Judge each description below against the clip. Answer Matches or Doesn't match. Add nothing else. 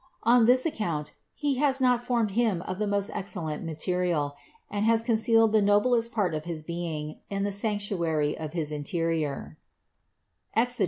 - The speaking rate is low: Doesn't match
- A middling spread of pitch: Doesn't match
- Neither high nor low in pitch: Doesn't match